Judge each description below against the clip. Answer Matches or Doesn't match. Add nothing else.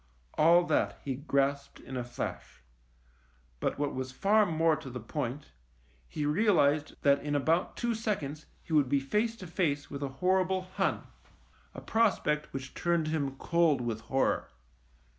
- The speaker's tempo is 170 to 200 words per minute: Doesn't match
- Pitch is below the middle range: Doesn't match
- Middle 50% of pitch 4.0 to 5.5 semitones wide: Matches